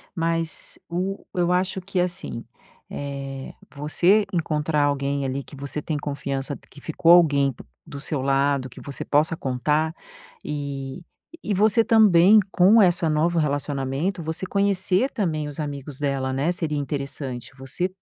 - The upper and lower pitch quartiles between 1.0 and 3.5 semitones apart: No, average, 4.2 semitones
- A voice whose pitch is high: No, medium, 150 Hz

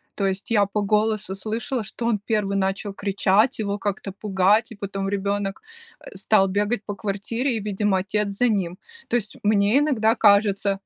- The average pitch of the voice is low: No, high, 205 Hz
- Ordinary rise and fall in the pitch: No, narrow, 1.8 semitones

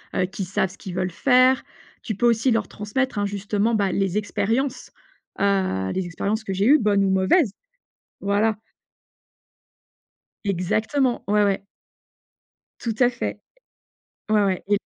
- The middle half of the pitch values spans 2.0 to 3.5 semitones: Yes, average, 2.9 semitones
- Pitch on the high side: Yes, high, 205 Hz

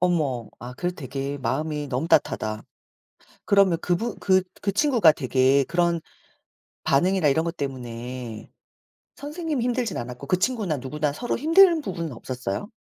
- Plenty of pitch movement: Yes, wide, 7.2 semitones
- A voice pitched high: No, medium, 160 Hz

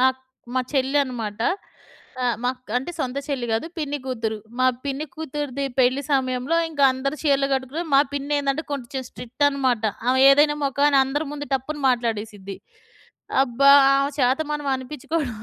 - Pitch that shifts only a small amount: Yes, narrow, 2.3 semitones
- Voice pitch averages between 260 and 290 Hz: Yes, very high, 270 Hz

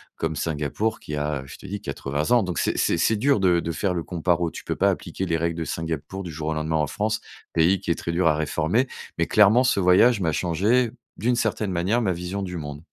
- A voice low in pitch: Yes, very low, 85 Hz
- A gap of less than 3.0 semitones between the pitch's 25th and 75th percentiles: No, average, 4.2 semitones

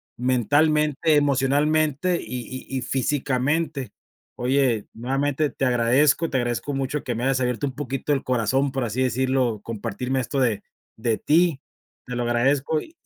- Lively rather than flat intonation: No, average, 2.7 semitones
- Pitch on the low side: Yes, low, 130 Hz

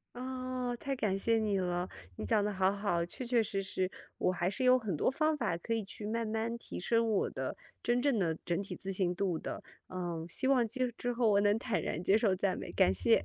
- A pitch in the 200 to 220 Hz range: Yes, high, 210 Hz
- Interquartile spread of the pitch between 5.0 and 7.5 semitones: No, average, 4.5 semitones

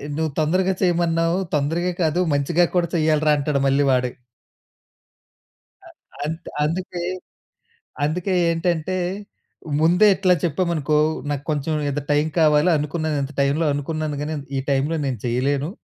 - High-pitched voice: No, medium, 155 Hz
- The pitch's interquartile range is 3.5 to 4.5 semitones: No, average, 2.9 semitones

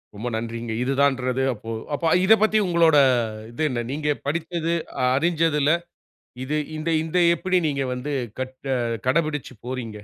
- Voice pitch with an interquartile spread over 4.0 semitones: Yes, average, 4.5 semitones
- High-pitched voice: No, medium, 140 Hz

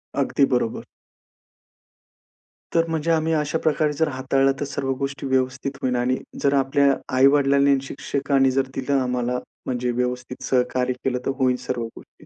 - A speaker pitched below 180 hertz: Yes, low, 135 Hz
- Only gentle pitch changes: Yes, narrow, 1.7 semitones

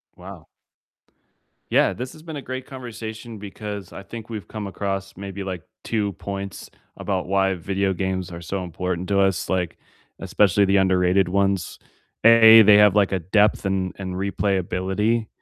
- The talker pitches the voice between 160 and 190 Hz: No, low, 100 Hz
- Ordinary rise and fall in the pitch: No, narrow, 2.1 semitones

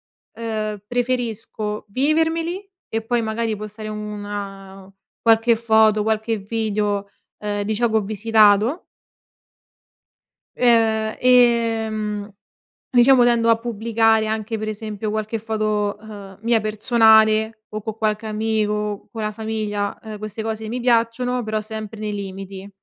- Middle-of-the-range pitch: No, high, 220 Hz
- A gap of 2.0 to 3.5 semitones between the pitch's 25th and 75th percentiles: No, narrow, 1.5 semitones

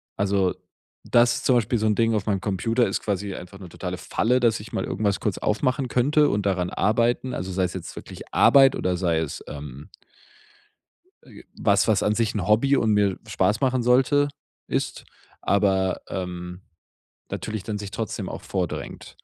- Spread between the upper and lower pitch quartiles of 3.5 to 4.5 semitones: Yes, average, 4.0 semitones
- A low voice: Yes, low, 105 Hz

